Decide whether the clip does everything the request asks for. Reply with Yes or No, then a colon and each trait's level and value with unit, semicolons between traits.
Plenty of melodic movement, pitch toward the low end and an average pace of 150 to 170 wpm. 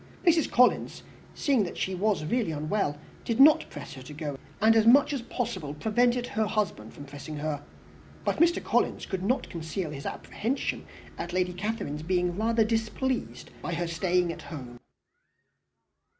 No: wide, 6.9 semitones; high, 190 Hz; average, 165 wpm